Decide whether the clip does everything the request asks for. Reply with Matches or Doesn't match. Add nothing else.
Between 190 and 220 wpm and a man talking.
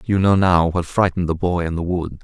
Doesn't match